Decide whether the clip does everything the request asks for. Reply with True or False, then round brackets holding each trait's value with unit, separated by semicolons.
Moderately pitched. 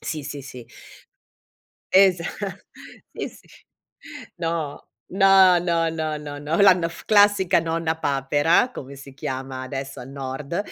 True (160 Hz)